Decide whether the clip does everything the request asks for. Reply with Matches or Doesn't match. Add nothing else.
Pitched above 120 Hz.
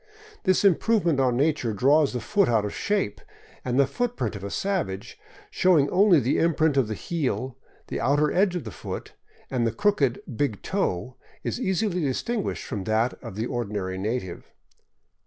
Matches